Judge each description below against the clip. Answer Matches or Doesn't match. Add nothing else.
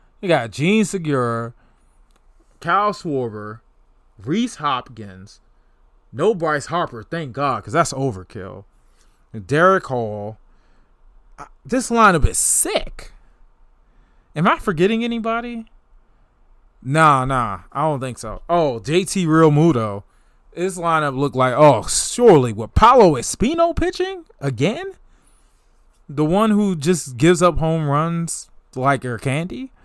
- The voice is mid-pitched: Matches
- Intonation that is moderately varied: Doesn't match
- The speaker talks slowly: Matches